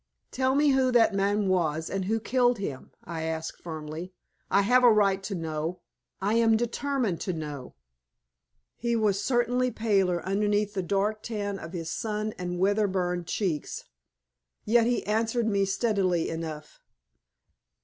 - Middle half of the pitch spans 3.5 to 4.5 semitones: Yes, average, 4.2 semitones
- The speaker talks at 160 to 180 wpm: No, average, 150 wpm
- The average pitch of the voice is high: Yes, high, 200 Hz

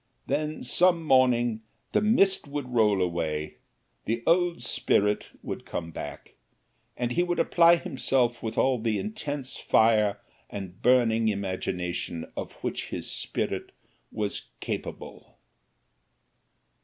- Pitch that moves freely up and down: Yes, wide, 6.2 semitones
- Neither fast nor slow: No, slow, 120 wpm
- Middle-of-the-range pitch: No, low, 120 Hz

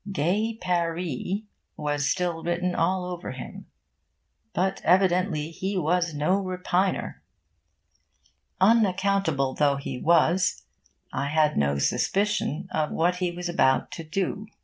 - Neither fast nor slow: No, slow, 120 wpm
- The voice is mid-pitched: Yes, medium, 175 Hz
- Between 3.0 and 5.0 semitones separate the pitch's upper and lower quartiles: Yes, average, 3.4 semitones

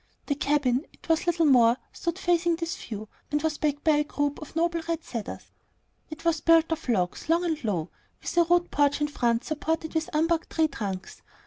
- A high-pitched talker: Yes, very high, 310 Hz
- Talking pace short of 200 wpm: No, fast, 205 wpm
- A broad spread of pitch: No, average, 3.3 semitones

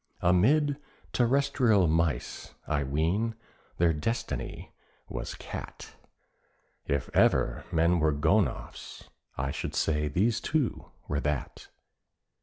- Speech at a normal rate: No, slow, 100 wpm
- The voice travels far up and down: Yes, wide, 7.3 semitones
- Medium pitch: No, very low, 85 Hz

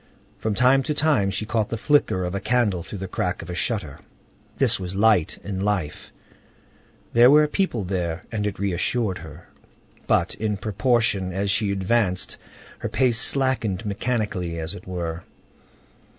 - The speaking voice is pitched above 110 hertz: No, low, 100 Hz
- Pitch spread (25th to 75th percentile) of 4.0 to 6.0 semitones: Yes, average, 4.3 semitones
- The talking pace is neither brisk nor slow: Yes, average, 155 wpm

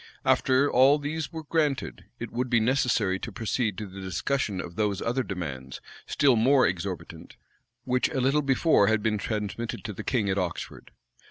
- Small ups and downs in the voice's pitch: No, average, 5.2 semitones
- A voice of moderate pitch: No, low, 115 Hz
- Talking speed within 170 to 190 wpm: Yes, average, 175 wpm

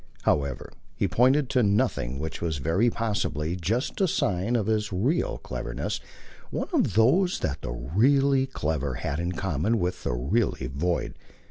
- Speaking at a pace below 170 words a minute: Yes, average, 155 wpm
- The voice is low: Yes, very low, 95 Hz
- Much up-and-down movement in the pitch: Yes, wide, 7.7 semitones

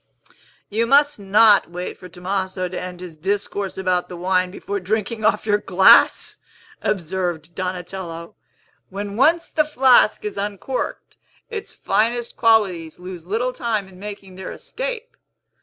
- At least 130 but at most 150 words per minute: Yes, average, 140 wpm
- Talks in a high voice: Yes, high, 195 Hz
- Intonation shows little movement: No, average, 3.5 semitones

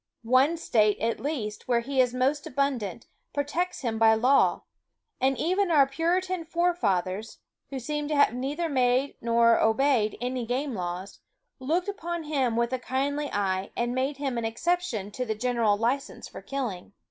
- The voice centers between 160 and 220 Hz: No, very high, 255 Hz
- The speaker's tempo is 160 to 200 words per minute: Yes, average, 165 wpm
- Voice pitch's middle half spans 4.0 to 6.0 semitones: Yes, average, 4.4 semitones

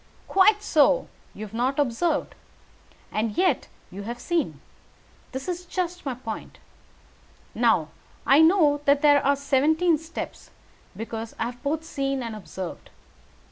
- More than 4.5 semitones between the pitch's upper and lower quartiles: Yes, wide, 5.6 semitones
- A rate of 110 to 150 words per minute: Yes, slow, 135 wpm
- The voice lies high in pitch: Yes, very high, 280 Hz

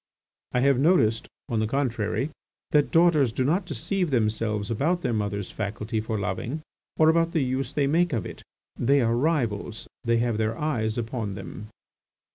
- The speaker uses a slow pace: No, average, 170 wpm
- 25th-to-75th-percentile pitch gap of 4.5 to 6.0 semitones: Yes, average, 5.3 semitones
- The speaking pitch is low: Yes, low, 120 Hz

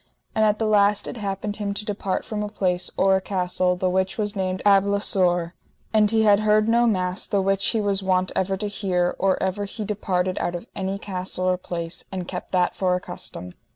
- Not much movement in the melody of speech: Yes, narrow, 2.1 semitones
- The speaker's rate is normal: No, fast, 220 wpm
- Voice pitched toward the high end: Yes, high, 195 Hz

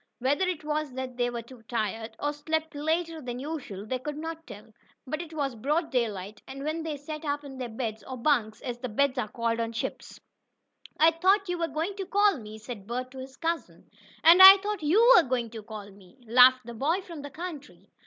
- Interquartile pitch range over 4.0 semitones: Yes, wide, 5.4 semitones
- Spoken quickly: Yes, fast, 215 wpm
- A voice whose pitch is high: Yes, very high, 275 Hz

